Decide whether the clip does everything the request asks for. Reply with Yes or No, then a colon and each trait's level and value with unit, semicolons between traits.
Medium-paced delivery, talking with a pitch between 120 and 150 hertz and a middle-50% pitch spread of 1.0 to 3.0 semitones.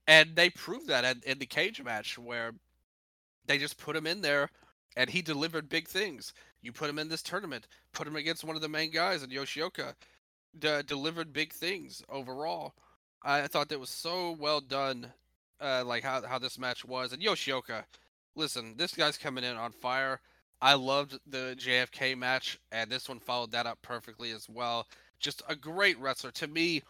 No: average, 190 wpm; low, 135 Hz; average, 3.9 semitones